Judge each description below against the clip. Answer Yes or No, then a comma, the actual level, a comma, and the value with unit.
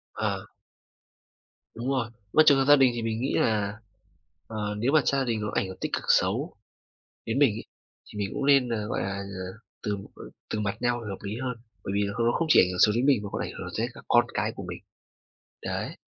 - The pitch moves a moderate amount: Yes, average, 3.9 semitones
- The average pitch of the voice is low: Yes, low, 110 Hz